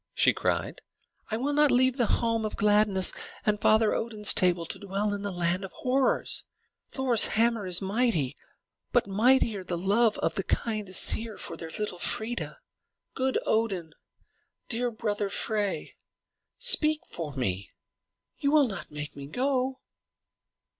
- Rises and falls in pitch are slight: No, average, 4.3 semitones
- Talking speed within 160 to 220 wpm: No, average, 145 wpm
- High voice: Yes, high, 215 Hz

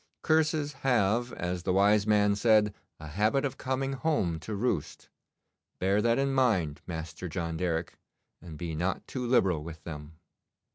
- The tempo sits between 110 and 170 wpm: Yes, average, 155 wpm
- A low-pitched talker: Yes, low, 100 Hz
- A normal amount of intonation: No, wide, 6.7 semitones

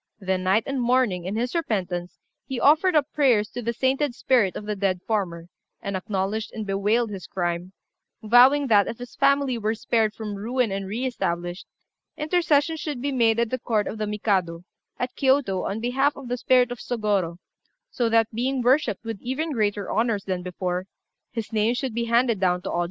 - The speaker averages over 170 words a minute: Yes, average, 195 wpm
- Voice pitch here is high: Yes, high, 225 Hz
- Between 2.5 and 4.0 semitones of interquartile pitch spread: No, average, 4.5 semitones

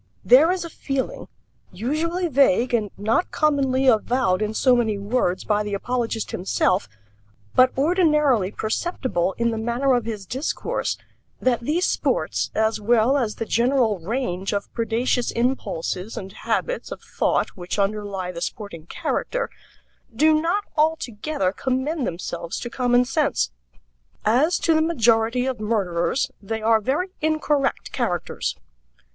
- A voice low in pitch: No, high, 240 Hz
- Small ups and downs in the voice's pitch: No, average, 4.9 semitones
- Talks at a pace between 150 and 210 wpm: No, average, 140 wpm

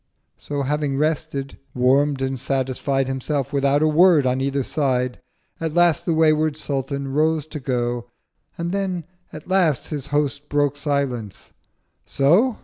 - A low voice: No, medium, 145 Hz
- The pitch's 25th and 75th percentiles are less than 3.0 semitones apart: Yes, narrow, 2.6 semitones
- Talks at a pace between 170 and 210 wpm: No, average, 140 wpm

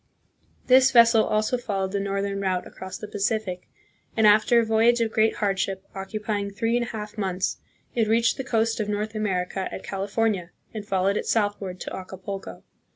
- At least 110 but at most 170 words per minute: No, average, 180 wpm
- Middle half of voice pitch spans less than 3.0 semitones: Yes, narrow, 2.5 semitones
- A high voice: Yes, high, 210 Hz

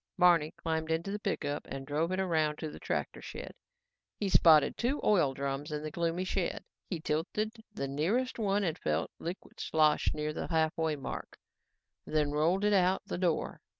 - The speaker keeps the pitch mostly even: No, average, 3.9 semitones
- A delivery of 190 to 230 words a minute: No, average, 180 wpm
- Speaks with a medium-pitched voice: Yes, medium, 160 Hz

